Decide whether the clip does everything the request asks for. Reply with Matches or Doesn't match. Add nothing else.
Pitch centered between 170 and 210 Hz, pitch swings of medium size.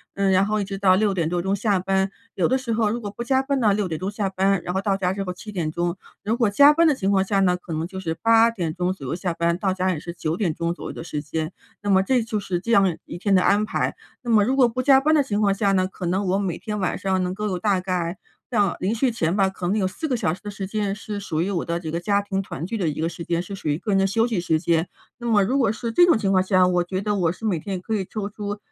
Matches